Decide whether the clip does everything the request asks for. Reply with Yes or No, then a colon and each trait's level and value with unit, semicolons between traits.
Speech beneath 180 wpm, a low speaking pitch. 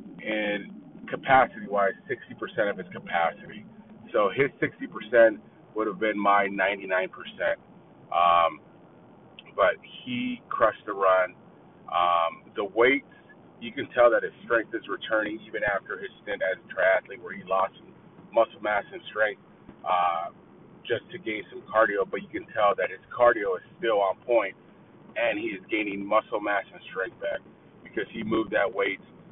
Yes: average, 160 wpm; low, 110 Hz